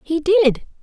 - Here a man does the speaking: No, female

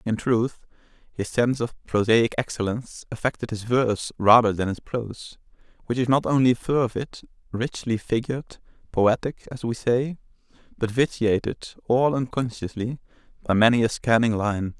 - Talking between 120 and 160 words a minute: Yes, average, 140 wpm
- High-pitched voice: No, low, 120 Hz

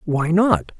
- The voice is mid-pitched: Yes, medium, 170 Hz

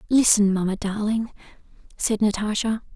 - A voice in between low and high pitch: No, high, 210 Hz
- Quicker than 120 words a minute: No, slow, 100 wpm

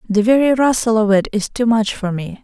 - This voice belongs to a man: No, female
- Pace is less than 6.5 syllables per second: Yes, 5.5 syllables/s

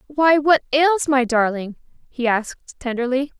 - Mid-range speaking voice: No, very high, 265 Hz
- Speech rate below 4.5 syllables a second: Yes, 4.3 syllables/s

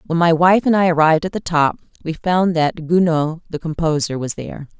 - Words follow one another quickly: Yes, fast, 215 wpm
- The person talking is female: Yes, female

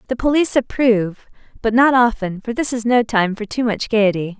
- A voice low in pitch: No, high, 230 Hz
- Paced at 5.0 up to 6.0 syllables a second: Yes, 5.5 syllables/s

